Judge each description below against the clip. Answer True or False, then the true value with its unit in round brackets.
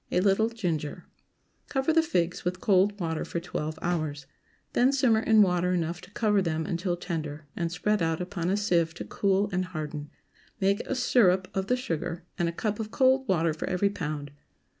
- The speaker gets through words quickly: False (190 wpm)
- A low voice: False (180 Hz)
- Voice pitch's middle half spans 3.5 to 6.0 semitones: True (3.9 semitones)